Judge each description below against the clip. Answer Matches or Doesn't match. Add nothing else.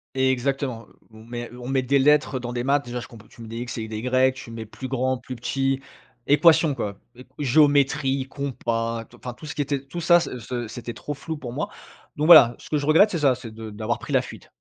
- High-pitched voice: Doesn't match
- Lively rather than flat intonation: Doesn't match